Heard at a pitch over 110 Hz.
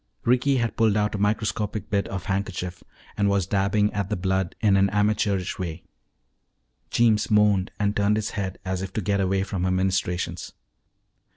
No: low, 100 Hz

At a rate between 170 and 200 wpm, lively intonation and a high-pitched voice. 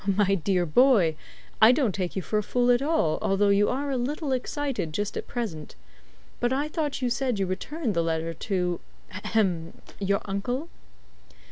Yes: average, 175 wpm; wide, 5.9 semitones; high, 210 Hz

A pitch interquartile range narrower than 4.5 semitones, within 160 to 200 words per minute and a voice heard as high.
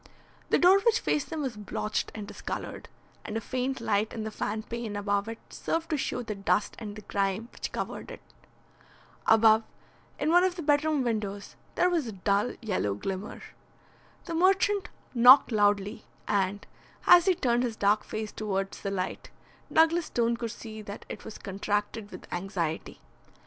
No: average, 5.2 semitones; average, 170 wpm; high, 220 Hz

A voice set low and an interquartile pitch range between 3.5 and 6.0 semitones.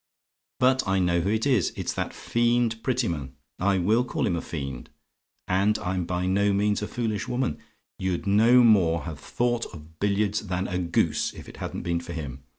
Yes: low, 100 Hz; average, 4.6 semitones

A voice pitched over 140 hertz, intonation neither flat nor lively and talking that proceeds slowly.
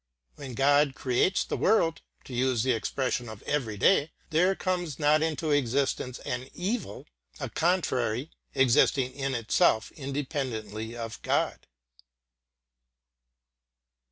No: low, 135 Hz; average, 4.2 semitones; slow, 115 wpm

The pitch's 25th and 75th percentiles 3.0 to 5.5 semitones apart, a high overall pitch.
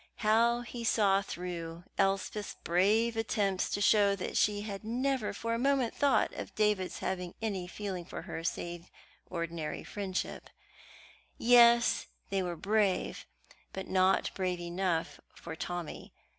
Yes: average, 3.8 semitones; high, 195 Hz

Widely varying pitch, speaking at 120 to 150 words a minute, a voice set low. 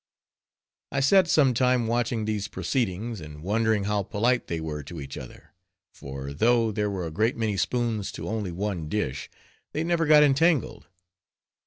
No: wide, 5.7 semitones; average, 165 wpm; low, 110 Hz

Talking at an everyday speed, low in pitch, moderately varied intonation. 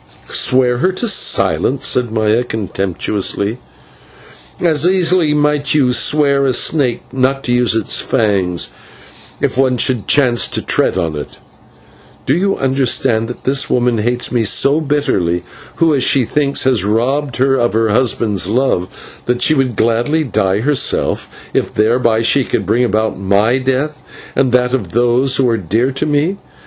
Yes: average, 155 wpm; low, 125 Hz; average, 3.7 semitones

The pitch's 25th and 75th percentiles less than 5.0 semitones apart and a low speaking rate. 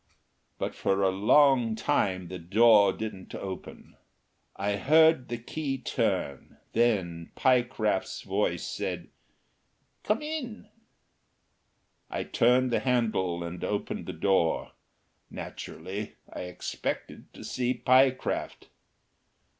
No: average, 5.3 semitones; slow, 105 wpm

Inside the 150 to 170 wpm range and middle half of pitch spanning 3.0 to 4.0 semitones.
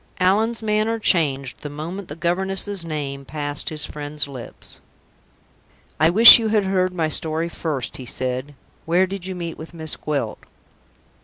No: average, 155 wpm; average, 4.5 semitones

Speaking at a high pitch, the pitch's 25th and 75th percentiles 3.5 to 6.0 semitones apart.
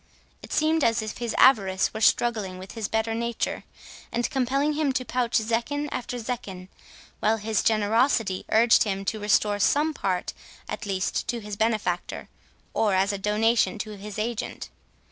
No: high, 220 Hz; average, 2.8 semitones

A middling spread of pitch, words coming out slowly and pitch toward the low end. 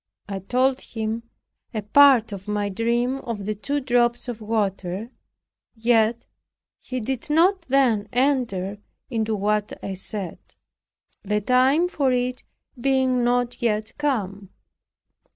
No: average, 3.5 semitones; slow, 125 wpm; high, 235 Hz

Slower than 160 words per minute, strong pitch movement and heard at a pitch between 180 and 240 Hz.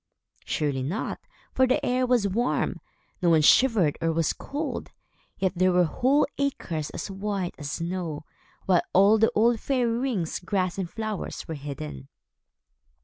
Yes: average, 150 wpm; wide, 6.0 semitones; medium, 185 Hz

